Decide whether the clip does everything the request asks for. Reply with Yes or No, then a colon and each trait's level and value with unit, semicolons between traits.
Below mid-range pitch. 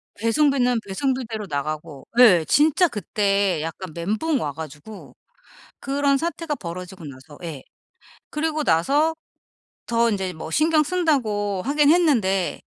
No: high, 215 Hz